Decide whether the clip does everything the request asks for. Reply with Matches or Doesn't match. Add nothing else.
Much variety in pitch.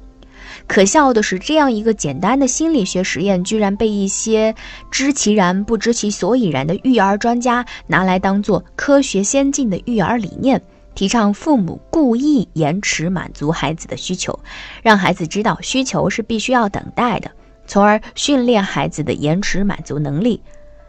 Doesn't match